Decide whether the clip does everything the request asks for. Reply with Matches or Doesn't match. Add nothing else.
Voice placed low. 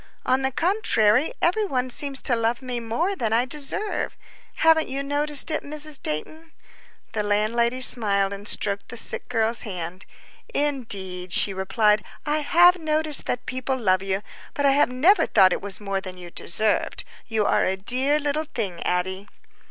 Doesn't match